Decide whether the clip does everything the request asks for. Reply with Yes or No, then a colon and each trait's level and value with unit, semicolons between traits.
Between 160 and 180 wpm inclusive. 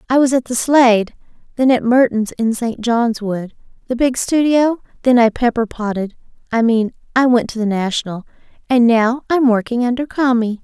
Yes: average, 170 wpm